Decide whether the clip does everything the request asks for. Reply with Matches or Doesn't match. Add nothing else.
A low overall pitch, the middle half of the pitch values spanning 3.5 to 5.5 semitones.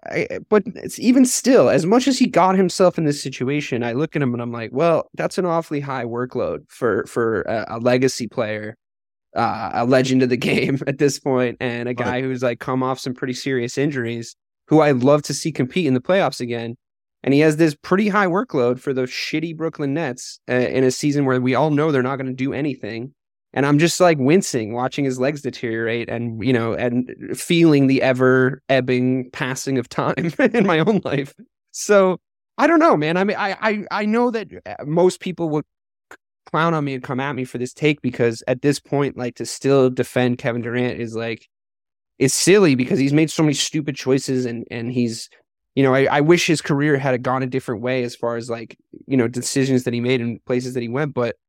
Matches